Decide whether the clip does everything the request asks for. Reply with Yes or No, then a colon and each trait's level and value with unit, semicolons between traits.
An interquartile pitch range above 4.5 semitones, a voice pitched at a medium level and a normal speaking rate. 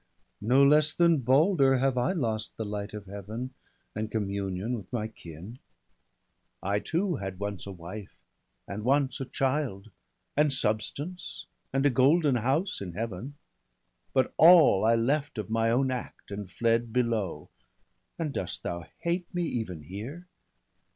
No: average, 5.3 semitones; low, 115 Hz; average, 150 wpm